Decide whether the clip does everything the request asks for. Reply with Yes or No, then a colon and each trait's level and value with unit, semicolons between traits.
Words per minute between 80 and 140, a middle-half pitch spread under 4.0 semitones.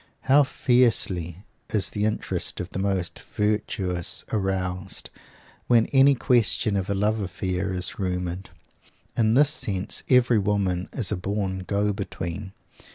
Yes: slow, 135 wpm; average, 2.8 semitones